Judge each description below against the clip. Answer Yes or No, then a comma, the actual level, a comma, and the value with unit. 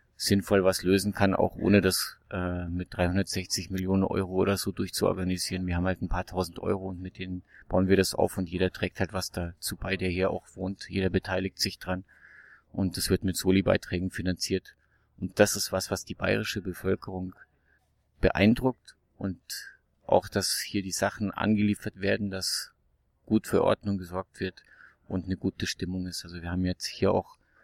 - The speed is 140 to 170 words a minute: No, average, 180 wpm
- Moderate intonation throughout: No, narrow, 1.4 semitones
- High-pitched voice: No, very low, 95 Hz